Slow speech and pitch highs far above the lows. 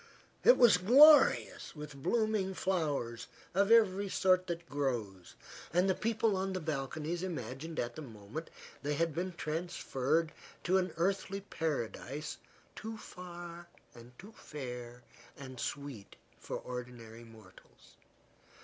Yes: slow, 115 wpm; wide, 6.6 semitones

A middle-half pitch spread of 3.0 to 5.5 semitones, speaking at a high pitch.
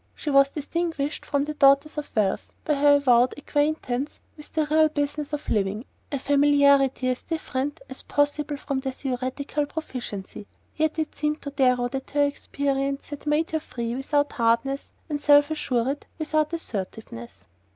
No: narrow, 2.5 semitones; very high, 285 Hz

